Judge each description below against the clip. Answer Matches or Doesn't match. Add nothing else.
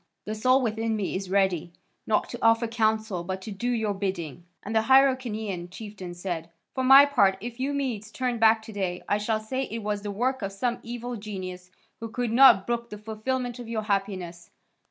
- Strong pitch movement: Doesn't match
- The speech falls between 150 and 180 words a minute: Doesn't match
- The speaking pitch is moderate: Doesn't match